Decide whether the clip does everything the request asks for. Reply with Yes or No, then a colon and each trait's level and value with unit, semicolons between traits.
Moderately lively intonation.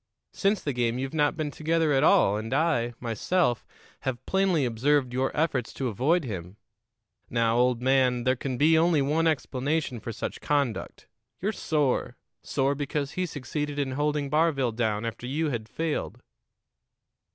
Yes: average, 4.1 semitones